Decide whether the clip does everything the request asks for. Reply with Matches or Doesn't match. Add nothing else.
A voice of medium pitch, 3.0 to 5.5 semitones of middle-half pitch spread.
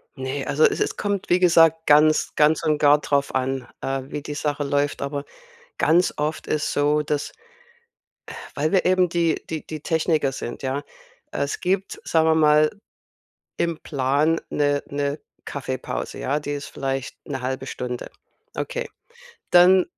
Doesn't match